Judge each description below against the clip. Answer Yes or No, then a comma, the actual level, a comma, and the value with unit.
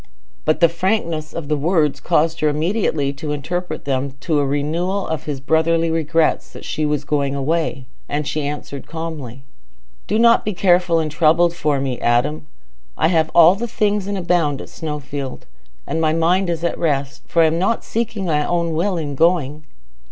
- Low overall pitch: No, medium, 160 Hz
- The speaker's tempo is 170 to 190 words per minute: Yes, average, 180 wpm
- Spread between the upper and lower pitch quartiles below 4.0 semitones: Yes, average, 2.9 semitones